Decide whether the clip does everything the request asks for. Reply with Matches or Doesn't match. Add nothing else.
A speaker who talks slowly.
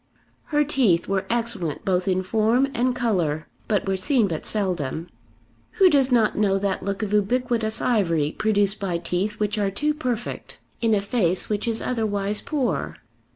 Doesn't match